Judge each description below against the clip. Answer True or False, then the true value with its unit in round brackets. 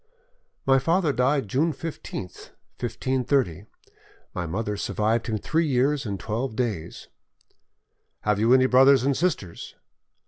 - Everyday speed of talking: False (125 wpm)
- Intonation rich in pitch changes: False (4.5 semitones)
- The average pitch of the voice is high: False (125 Hz)